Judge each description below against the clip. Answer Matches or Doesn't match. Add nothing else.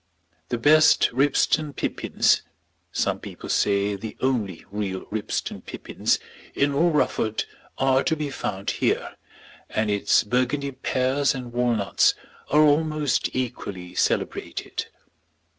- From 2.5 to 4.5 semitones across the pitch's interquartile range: Doesn't match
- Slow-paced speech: Matches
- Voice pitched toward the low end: Matches